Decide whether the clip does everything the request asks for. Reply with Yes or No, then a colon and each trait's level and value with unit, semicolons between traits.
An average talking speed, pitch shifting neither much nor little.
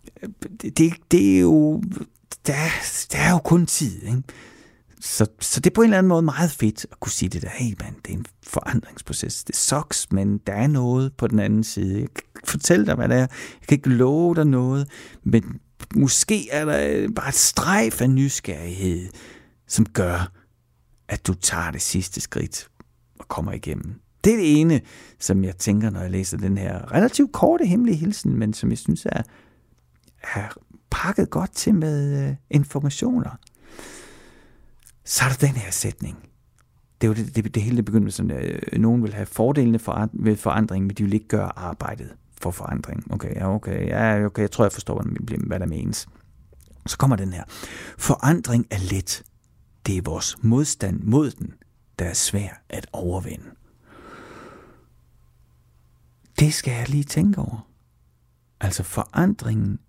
No: average, 170 wpm; wide, 6.4 semitones